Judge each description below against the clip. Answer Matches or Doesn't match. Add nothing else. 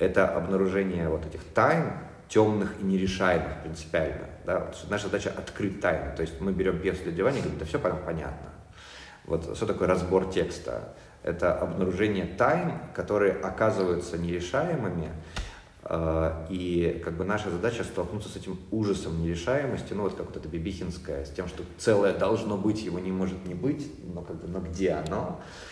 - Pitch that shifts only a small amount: Matches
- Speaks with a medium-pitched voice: Doesn't match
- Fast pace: Matches